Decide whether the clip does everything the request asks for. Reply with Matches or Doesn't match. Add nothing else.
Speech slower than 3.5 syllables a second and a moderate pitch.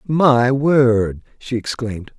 Doesn't match